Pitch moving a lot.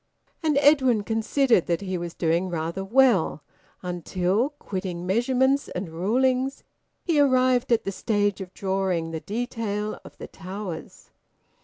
Yes: wide, 5.9 semitones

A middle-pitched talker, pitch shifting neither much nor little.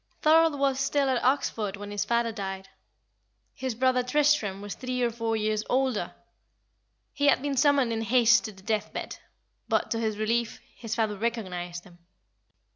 No: high, 230 Hz; average, 3.7 semitones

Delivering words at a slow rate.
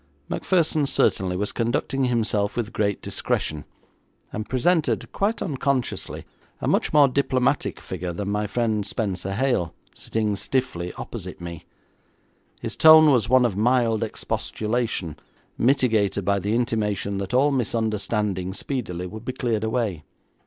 Yes: slow, 130 wpm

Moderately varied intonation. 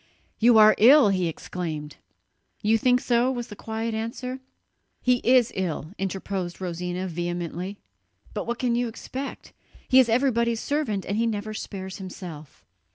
Yes: average, 4.6 semitones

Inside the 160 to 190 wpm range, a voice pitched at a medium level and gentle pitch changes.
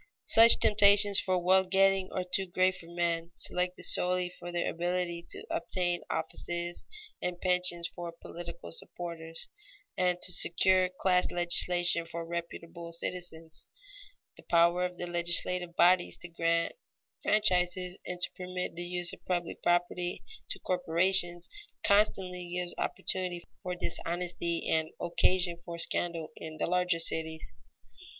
No: slow, 135 wpm; medium, 175 Hz; narrow, 1.2 semitones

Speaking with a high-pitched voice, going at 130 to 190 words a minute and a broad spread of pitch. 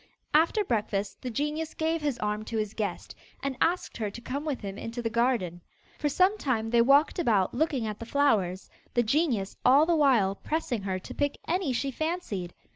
No: very high, 250 Hz; average, 200 wpm; wide, 6.0 semitones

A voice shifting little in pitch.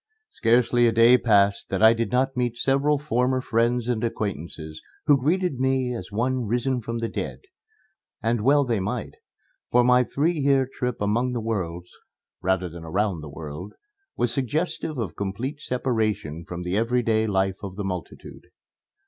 No: average, 4.2 semitones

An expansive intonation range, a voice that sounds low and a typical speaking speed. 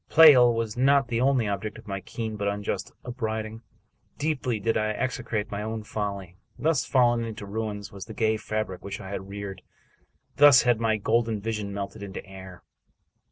No: average, 2.8 semitones; low, 110 Hz; average, 175 wpm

